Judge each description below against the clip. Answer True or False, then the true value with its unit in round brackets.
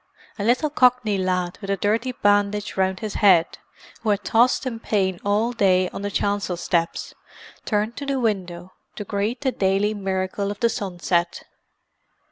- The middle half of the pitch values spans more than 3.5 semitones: False (3.1 semitones)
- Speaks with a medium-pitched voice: False (205 Hz)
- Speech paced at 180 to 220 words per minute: False (165 wpm)